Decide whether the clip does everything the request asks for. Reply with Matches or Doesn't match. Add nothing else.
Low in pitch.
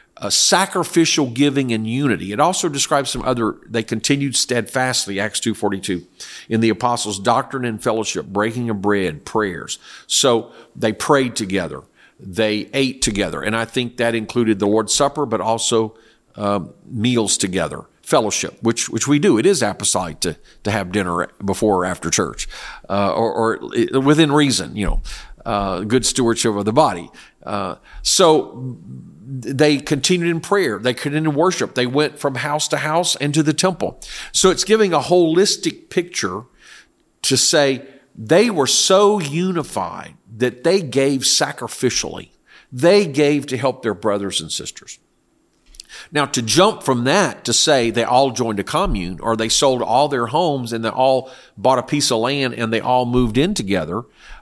Matches